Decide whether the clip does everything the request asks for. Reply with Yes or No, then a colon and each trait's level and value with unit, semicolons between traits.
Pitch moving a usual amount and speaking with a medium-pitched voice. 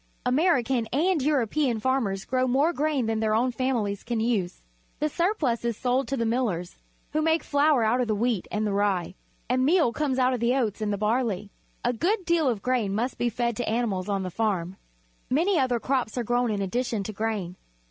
No: average, 3.7 semitones; high, 240 Hz